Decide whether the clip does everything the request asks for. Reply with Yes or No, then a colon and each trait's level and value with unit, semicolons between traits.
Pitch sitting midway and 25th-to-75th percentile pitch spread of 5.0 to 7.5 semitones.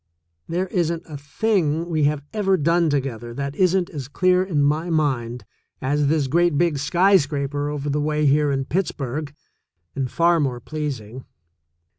No: medium, 150 Hz; average, 3.4 semitones